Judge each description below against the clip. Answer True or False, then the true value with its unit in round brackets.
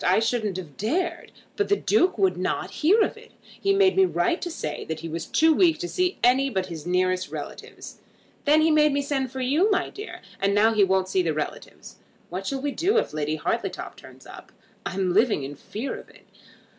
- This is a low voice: False (240 Hz)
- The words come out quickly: True (220 wpm)